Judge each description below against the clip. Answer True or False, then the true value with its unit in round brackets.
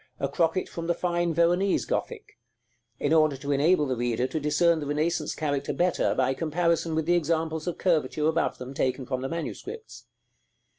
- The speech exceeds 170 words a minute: True (180 wpm)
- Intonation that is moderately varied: True (3.1 semitones)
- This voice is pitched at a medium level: True (160 Hz)